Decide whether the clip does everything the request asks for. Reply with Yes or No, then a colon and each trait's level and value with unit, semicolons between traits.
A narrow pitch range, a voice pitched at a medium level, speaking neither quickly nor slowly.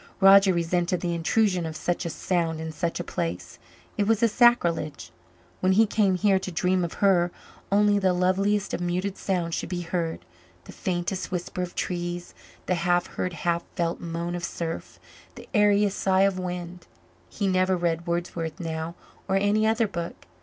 Yes: narrow, 2.3 semitones; medium, 180 Hz; average, 175 wpm